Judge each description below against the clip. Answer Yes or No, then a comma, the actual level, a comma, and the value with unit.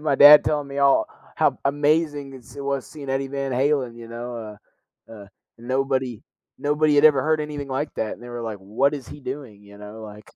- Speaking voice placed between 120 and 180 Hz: Yes, low, 135 Hz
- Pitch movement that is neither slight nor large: Yes, average, 3.7 semitones